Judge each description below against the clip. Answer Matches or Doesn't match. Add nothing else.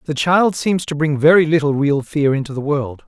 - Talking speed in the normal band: Doesn't match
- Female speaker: Doesn't match